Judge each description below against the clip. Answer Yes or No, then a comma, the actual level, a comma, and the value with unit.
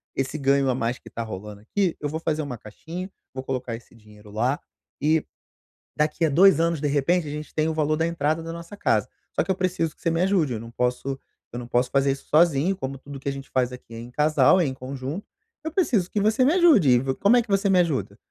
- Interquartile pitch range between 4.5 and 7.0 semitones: Yes, average, 4.9 semitones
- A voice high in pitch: No, medium, 150 Hz